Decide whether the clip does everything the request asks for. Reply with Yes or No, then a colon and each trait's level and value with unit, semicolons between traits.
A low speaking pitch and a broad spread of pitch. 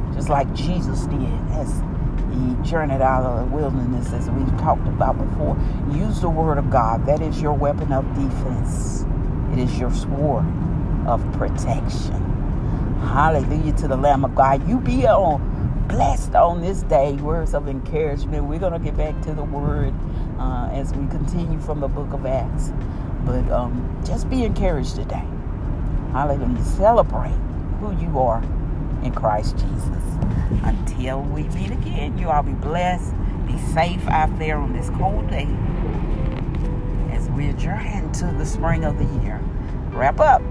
Yes: low, 125 Hz; wide, 7.8 semitones